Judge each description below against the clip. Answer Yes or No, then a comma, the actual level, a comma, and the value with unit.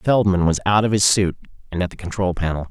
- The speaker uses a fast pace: Yes, fast, 245 wpm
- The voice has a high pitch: No, very low, 95 Hz